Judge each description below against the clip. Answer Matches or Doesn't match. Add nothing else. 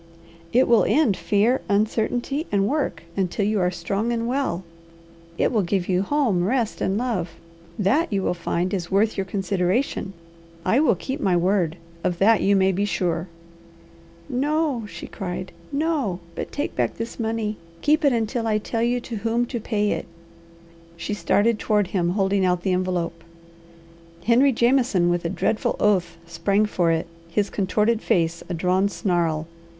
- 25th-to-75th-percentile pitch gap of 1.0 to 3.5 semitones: Doesn't match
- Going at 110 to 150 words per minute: Doesn't match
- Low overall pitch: Doesn't match